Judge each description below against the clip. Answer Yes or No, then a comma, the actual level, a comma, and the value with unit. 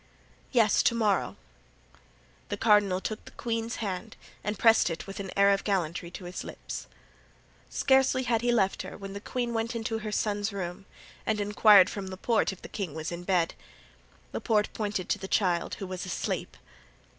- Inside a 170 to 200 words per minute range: Yes, average, 180 wpm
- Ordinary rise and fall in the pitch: Yes, average, 3.1 semitones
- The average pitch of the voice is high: Yes, high, 205 Hz